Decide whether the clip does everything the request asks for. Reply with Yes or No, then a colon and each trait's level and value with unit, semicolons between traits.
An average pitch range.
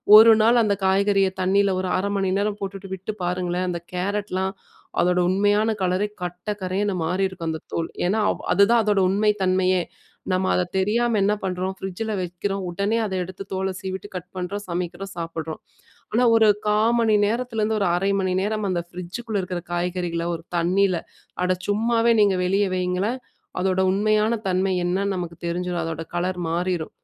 No: narrow, 2.3 semitones